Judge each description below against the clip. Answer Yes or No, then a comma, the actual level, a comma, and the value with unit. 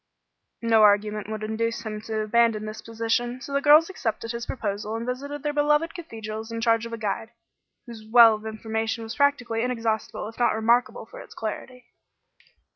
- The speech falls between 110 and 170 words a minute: No, average, 180 wpm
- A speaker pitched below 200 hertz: No, high, 230 Hz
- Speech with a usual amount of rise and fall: No, narrow, 2.2 semitones